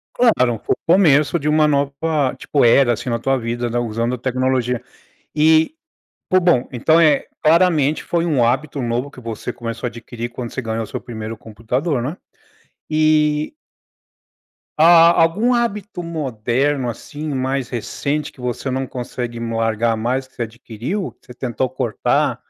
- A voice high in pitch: No, low, 130 Hz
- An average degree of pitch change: Yes, average, 4.6 semitones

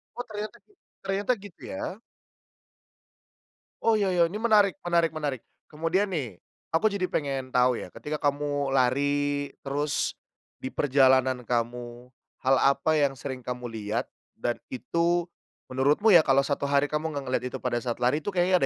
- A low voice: No, medium, 145 Hz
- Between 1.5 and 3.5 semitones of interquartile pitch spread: No, average, 5.0 semitones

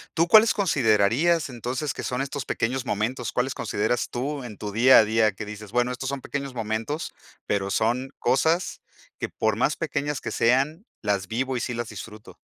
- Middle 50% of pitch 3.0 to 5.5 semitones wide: Yes, average, 4.1 semitones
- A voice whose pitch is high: No, low, 125 Hz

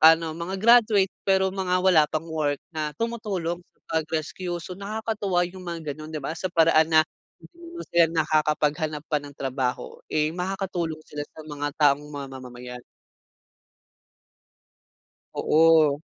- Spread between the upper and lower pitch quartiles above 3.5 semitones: Yes, average, 4.0 semitones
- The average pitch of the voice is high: No, medium, 160 Hz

